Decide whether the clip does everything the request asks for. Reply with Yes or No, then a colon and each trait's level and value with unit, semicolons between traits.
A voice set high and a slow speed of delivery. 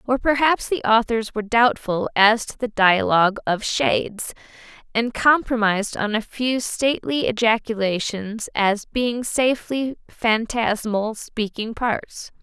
Yes: high, 225 Hz; slow, 120 wpm